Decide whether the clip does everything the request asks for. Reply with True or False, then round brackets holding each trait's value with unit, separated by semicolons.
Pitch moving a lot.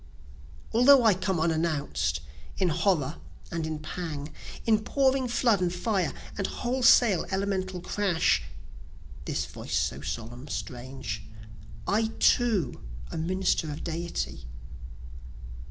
True (5.8 semitones)